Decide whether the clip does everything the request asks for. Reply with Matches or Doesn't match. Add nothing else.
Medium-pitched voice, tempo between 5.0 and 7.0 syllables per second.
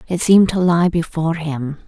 Matches